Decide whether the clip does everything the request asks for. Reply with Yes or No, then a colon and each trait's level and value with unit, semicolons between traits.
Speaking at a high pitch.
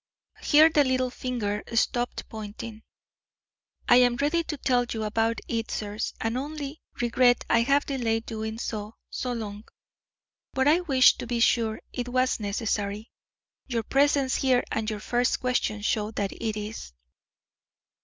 Yes: high, 235 Hz